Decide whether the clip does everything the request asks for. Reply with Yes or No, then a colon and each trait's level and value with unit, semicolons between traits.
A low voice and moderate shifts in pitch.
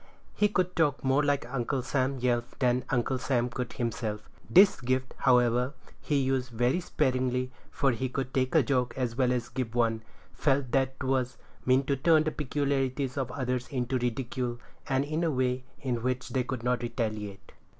No: low, 130 Hz; narrow, 1.8 semitones